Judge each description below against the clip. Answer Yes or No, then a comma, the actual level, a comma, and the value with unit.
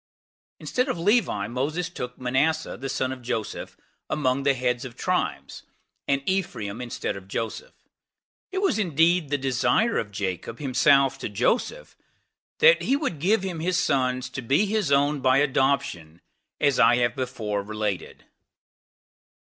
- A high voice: No, low, 135 Hz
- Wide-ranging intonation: Yes, wide, 5.9 semitones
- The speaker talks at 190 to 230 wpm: No, average, 150 wpm